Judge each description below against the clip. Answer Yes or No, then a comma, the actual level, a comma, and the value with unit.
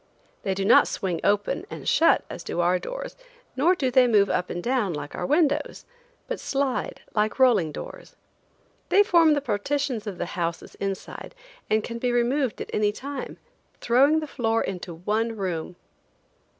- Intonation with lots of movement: Yes, wide, 6.4 semitones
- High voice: Yes, high, 230 Hz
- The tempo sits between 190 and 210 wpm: No, average, 170 wpm